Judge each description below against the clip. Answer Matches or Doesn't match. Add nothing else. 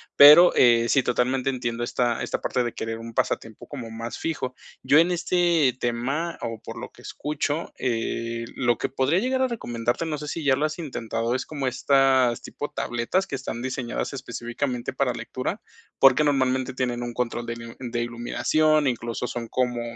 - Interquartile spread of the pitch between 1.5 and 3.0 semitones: Doesn't match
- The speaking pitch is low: Matches